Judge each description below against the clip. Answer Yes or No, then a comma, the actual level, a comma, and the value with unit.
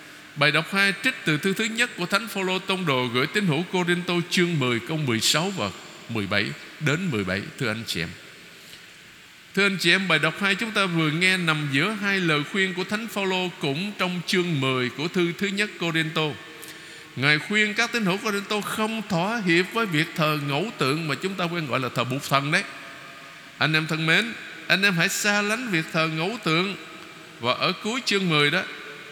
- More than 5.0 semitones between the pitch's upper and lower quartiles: No, average, 4.4 semitones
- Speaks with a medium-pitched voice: Yes, medium, 175 Hz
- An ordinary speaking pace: Yes, average, 210 wpm